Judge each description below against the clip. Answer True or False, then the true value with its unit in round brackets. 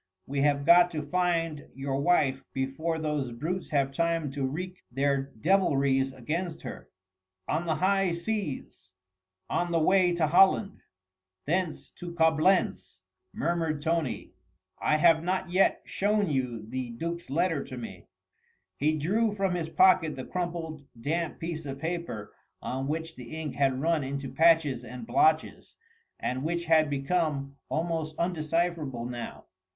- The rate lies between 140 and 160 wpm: True (145 wpm)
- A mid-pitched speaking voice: True (160 Hz)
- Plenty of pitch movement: False (3.9 semitones)